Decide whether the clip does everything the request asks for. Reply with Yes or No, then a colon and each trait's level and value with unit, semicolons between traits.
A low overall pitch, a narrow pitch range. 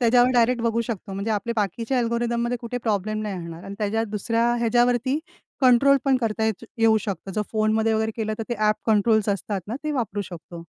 No: high, 225 Hz; narrow, 2.3 semitones